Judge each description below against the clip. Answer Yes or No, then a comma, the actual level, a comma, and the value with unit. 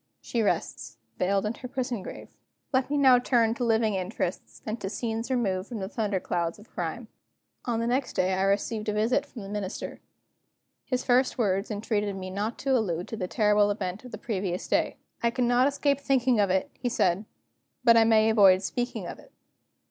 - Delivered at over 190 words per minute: Yes, average, 200 wpm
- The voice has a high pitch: Yes, high, 220 Hz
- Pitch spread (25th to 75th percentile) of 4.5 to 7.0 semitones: No, average, 3.8 semitones